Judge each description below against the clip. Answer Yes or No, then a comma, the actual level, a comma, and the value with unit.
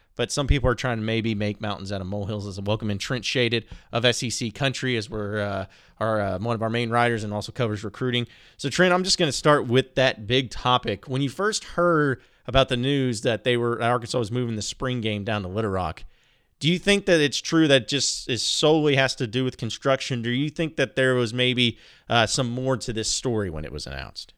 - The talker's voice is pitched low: Yes, low, 120 Hz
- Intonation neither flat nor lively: Yes, average, 3.6 semitones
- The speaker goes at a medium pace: No, fast, 240 wpm